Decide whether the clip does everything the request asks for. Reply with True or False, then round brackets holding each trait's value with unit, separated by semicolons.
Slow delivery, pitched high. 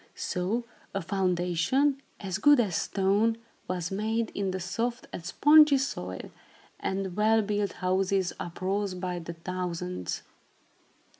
True (125 wpm; 195 Hz)